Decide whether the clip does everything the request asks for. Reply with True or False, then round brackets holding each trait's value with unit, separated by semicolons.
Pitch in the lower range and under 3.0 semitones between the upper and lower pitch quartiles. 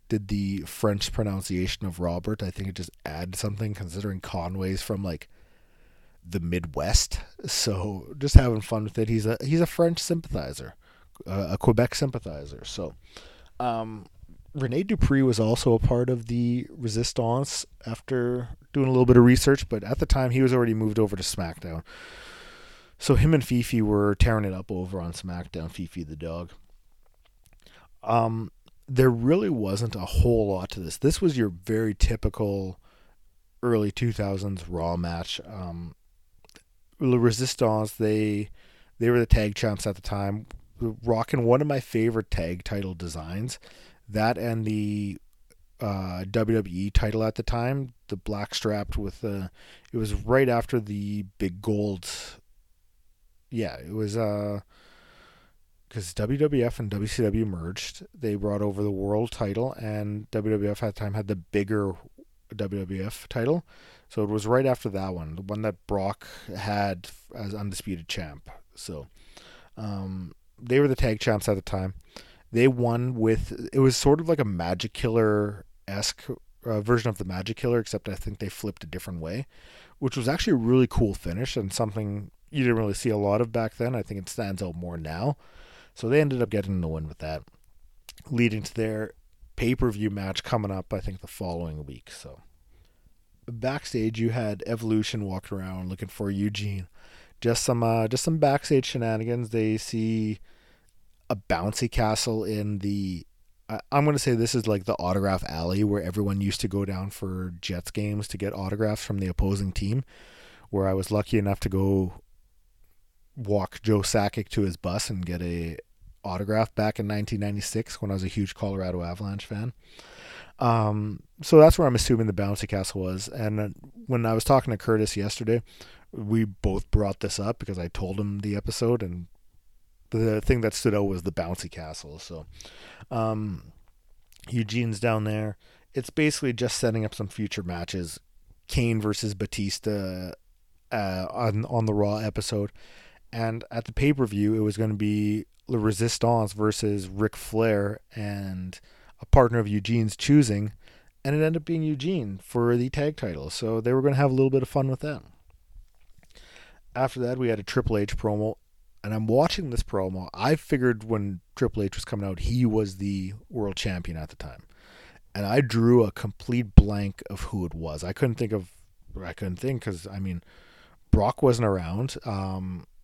False (105 Hz; 3.6 semitones)